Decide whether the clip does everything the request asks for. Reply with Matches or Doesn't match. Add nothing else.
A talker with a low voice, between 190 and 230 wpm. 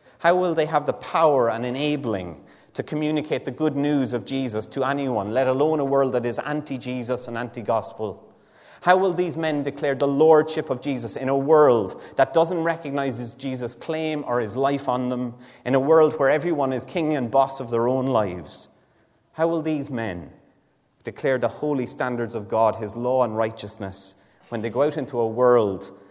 Matches